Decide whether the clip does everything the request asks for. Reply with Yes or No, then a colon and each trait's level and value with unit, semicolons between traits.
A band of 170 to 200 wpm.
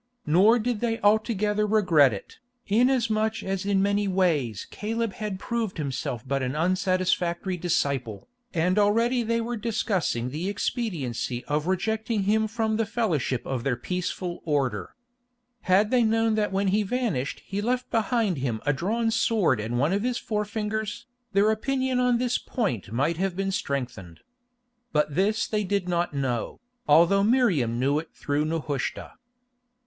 No: average, 155 wpm